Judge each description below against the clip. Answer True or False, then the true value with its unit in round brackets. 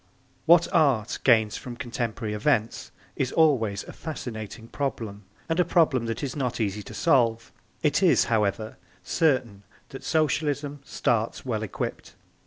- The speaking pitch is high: False (120 Hz)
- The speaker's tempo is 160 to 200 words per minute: False (140 wpm)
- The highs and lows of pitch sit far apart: False (4.8 semitones)